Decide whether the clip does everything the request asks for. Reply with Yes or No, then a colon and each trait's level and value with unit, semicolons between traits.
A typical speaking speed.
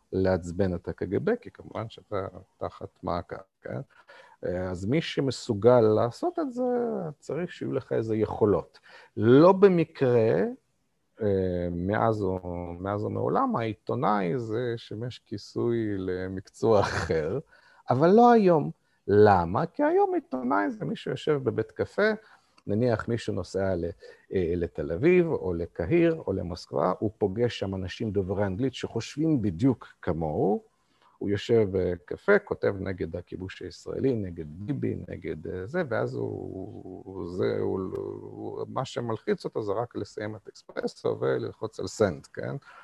Yes: average, 125 wpm